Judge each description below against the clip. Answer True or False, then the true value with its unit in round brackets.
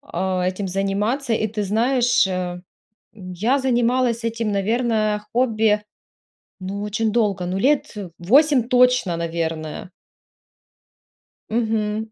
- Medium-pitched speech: False (215 Hz)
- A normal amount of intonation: True (3.9 semitones)